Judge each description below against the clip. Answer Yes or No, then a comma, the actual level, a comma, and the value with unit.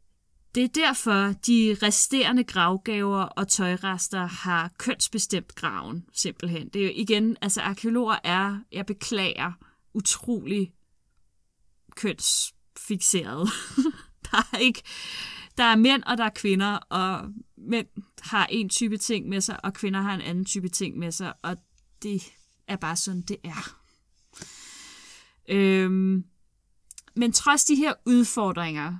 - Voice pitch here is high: Yes, high, 200 Hz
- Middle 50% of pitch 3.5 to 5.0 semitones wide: Yes, average, 3.8 semitones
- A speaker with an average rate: No, slow, 130 wpm